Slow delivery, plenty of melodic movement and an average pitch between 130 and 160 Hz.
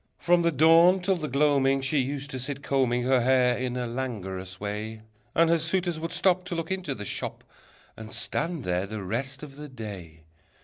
No: average, 195 wpm; wide, 6.0 semitones; low, 135 Hz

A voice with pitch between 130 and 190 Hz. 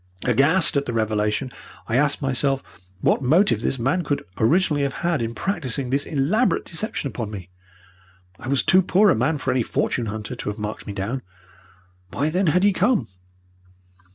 Yes: low, 135 Hz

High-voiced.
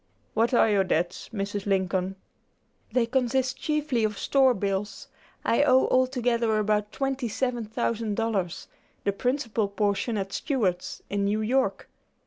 Yes: high, 220 Hz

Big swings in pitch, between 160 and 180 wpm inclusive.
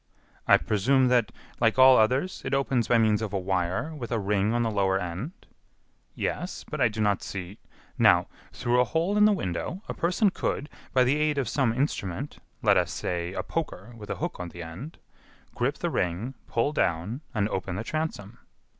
No: wide, 6.2 semitones; average, 200 wpm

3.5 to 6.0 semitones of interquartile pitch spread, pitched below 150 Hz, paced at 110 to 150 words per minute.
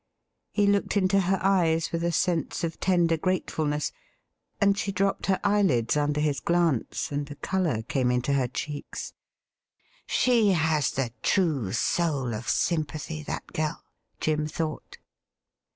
No: average, 4.4 semitones; medium, 160 Hz; average, 145 wpm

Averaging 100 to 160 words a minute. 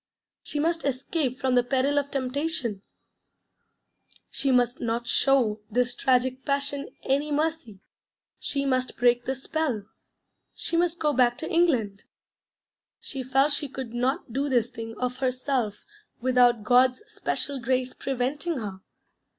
Yes: slow, 135 wpm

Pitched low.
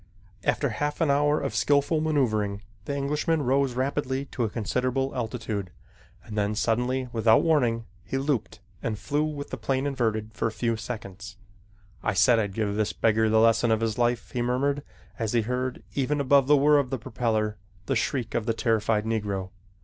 Yes: low, 120 Hz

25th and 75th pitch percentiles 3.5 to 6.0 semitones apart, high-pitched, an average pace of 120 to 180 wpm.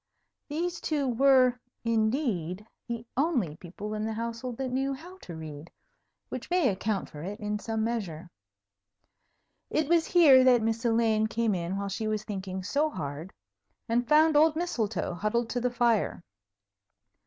Yes: average, 4.9 semitones; high, 230 Hz; average, 155 wpm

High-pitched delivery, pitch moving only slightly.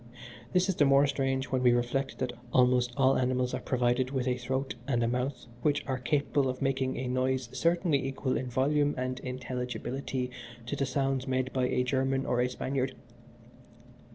No: low, 130 Hz; narrow, 1.3 semitones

